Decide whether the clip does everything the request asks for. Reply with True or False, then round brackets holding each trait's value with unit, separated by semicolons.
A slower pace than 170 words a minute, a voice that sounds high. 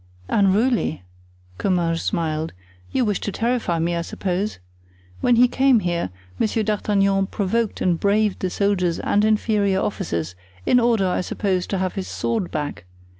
True (150 wpm; 195 Hz)